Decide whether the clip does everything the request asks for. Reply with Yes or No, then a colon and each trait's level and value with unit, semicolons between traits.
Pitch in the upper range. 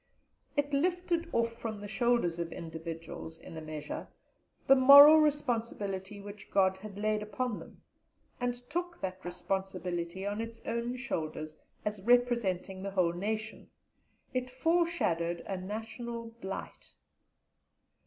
Yes: high, 210 Hz